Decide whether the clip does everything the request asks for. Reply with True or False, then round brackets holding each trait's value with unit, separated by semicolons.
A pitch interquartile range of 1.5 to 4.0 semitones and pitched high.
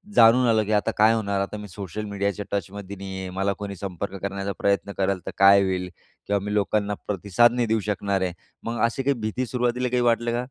False (2.5 semitones; 100 Hz)